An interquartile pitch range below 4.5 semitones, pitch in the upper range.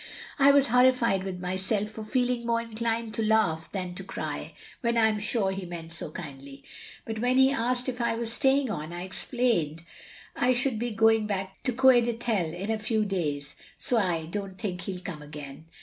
No: average, 4.8 semitones; high, 215 Hz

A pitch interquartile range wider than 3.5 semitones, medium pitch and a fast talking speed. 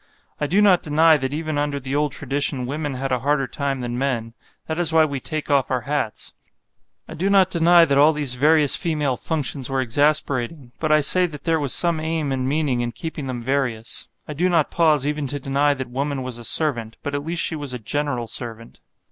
No: average, 3.2 semitones; medium, 145 Hz; fast, 225 wpm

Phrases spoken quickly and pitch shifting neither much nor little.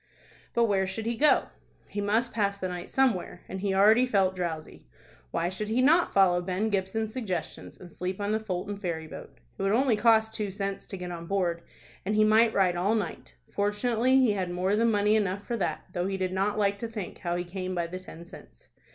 Yes: fast, 220 wpm; average, 3.1 semitones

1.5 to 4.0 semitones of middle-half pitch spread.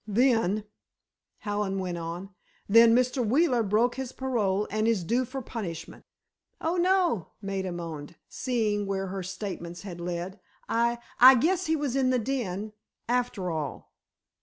No: average, 4.8 semitones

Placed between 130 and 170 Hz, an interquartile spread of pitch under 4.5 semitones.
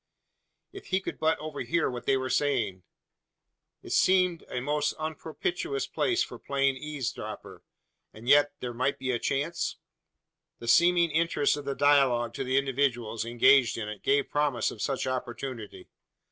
Yes: medium, 140 Hz; average, 4.1 semitones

